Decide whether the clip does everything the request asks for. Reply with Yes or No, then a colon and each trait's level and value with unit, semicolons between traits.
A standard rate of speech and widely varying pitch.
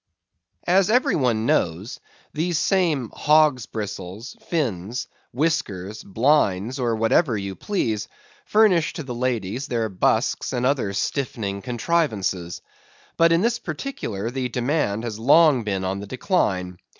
No: slow, 130 wpm; wide, 7.3 semitones